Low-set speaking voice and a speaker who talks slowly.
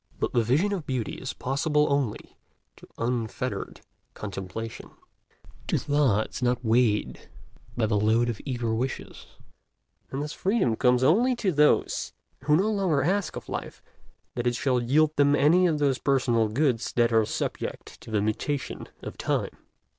No: low, 130 Hz; average, 155 wpm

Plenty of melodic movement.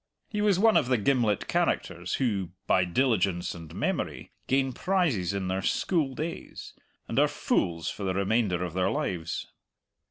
Yes: wide, 6.9 semitones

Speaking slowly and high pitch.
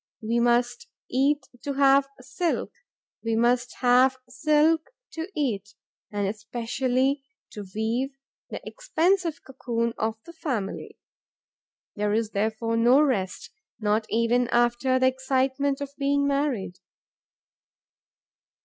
Yes: slow, 115 wpm; very high, 250 Hz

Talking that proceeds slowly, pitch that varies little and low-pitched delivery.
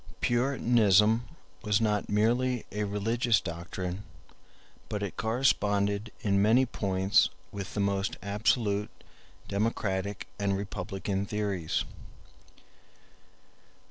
Yes: slow, 90 wpm; narrow, 2.3 semitones; low, 105 Hz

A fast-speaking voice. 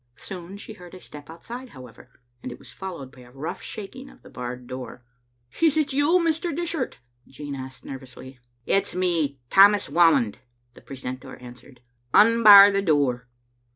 No: average, 170 wpm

